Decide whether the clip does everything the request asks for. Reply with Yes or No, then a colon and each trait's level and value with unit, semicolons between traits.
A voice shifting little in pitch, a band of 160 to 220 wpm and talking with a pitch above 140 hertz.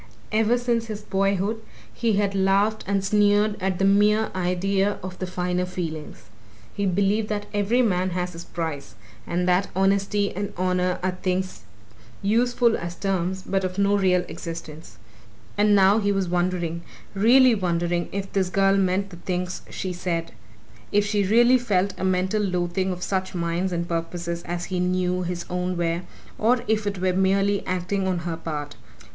Yes: narrow, 2.2 semitones; average, 170 wpm; high, 190 Hz